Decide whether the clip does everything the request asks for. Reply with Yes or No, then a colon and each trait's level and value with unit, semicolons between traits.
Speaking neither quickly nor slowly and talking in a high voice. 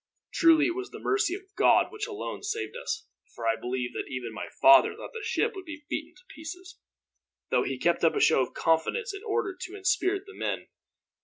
No: fast, 215 wpm; very high, 370 Hz